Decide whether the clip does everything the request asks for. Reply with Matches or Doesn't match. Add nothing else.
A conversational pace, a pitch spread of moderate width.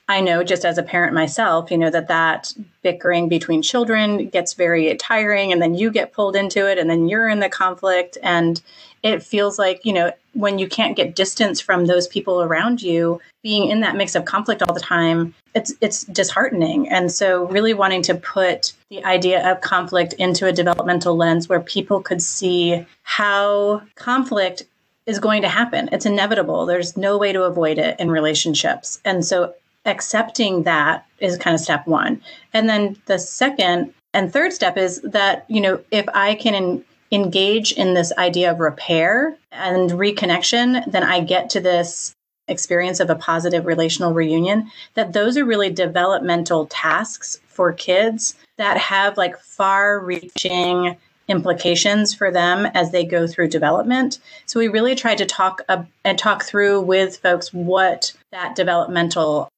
Matches